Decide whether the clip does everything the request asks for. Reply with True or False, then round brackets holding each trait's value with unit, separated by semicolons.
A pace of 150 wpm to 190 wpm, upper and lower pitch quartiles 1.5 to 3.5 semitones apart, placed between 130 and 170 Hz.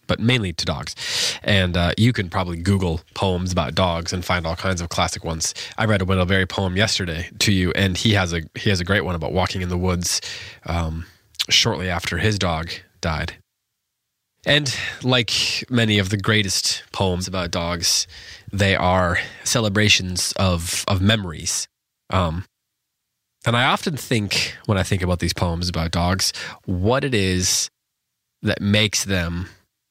False (165 wpm; 3.0 semitones; 95 Hz)